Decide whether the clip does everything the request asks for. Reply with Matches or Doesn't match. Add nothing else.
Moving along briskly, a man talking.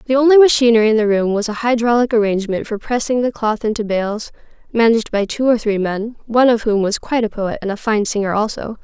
Doesn't match